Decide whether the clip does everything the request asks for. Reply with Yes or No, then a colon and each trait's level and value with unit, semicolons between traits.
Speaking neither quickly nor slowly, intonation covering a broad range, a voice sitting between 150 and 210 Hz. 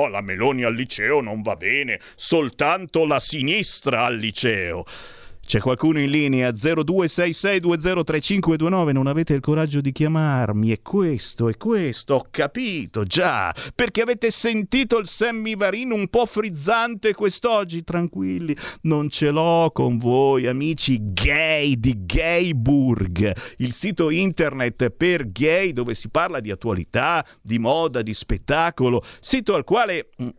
Yes: average, 130 wpm; wide, 6.8 semitones; medium, 155 Hz